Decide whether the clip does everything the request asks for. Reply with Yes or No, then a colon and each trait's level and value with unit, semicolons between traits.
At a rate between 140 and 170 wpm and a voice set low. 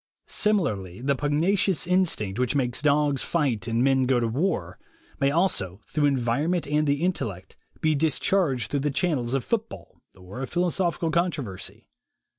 No: average, 150 wpm; medium, 145 Hz